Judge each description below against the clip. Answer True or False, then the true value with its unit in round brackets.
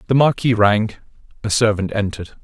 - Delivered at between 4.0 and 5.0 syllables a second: False (6.0 syllables/s)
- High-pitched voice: False (110 Hz)